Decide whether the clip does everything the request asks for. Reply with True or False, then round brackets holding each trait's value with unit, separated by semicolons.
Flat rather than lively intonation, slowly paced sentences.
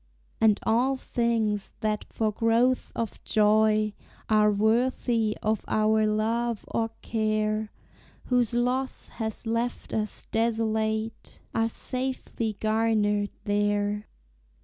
True (1.5 semitones; 105 wpm)